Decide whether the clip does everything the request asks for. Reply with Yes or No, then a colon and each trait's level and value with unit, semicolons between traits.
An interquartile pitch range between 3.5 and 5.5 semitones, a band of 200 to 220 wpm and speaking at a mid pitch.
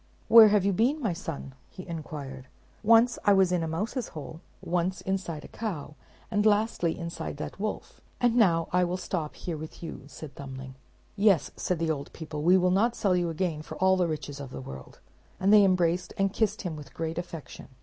Yes: average, 4.1 semitones; fast, 205 wpm; medium, 175 Hz